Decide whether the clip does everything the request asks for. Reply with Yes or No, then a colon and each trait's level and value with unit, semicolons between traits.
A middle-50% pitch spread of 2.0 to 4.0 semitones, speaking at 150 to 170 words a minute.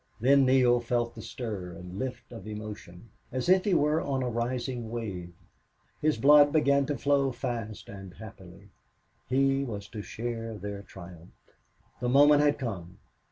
No: average, 5.0 semitones; average, 160 wpm